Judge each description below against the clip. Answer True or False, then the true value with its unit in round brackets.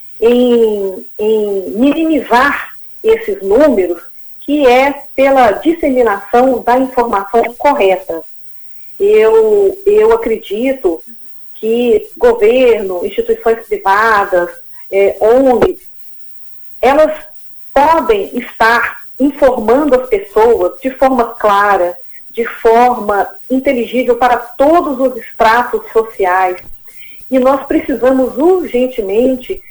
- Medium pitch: False (255 Hz)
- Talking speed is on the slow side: True (85 wpm)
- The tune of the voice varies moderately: False (6.2 semitones)